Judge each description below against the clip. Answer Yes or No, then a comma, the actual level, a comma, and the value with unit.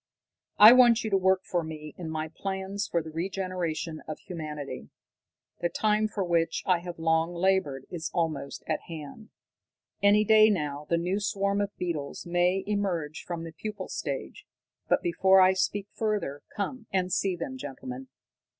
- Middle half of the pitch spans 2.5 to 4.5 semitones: Yes, average, 3.8 semitones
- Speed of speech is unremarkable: Yes, average, 165 wpm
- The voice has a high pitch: No, medium, 180 Hz